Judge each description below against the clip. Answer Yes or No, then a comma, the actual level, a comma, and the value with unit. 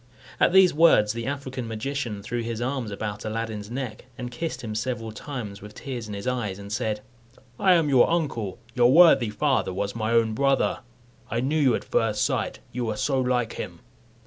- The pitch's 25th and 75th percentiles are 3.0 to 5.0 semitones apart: Yes, average, 3.9 semitones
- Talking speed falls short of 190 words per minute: No, average, 195 wpm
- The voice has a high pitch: No, low, 115 Hz